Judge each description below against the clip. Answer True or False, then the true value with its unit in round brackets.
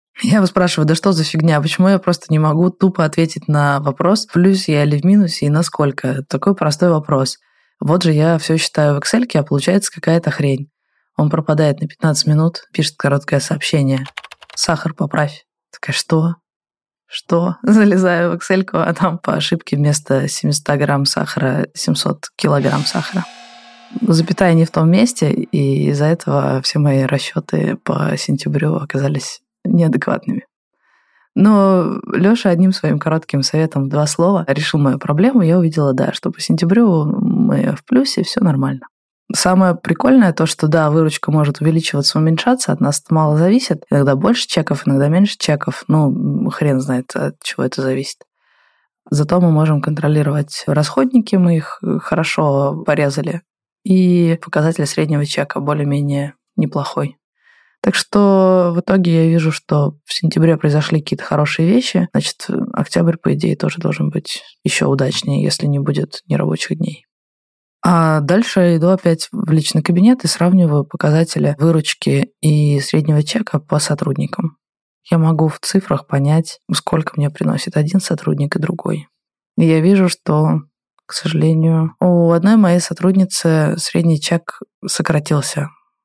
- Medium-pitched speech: True (165 Hz)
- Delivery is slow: False (145 wpm)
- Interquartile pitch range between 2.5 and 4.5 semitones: True (3.7 semitones)